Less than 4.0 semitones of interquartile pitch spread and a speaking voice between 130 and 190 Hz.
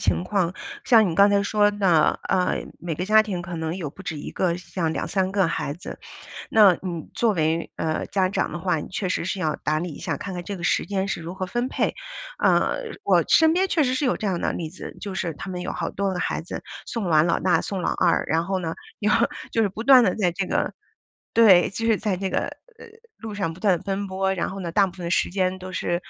Yes: average, 2.9 semitones; medium, 185 Hz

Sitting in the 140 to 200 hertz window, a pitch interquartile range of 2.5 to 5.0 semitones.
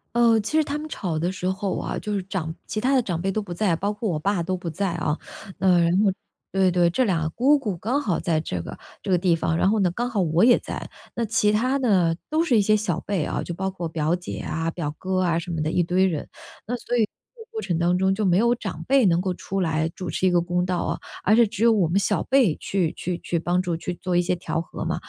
Yes: medium, 185 Hz; average, 3.9 semitones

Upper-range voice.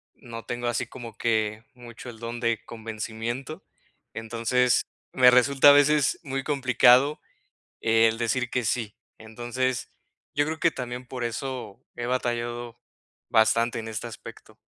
No: low, 120 Hz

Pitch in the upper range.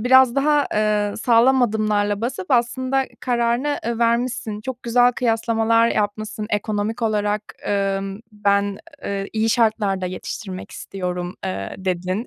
Yes: high, 215 Hz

